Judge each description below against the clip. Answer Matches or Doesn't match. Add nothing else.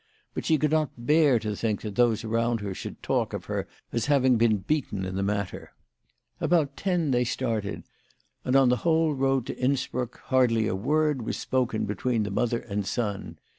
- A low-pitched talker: Matches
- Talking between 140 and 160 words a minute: Doesn't match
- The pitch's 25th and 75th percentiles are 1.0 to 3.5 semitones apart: Doesn't match